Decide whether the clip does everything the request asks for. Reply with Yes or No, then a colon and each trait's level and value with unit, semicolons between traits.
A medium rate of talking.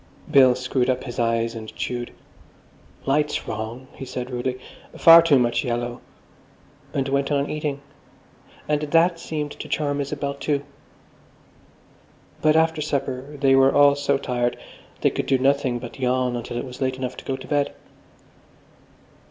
Yes: average, 155 wpm